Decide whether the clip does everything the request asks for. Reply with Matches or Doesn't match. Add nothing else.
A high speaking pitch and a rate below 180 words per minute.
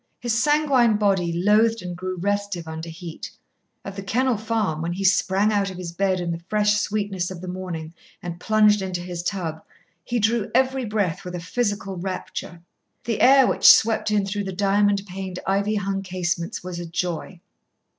Doesn't match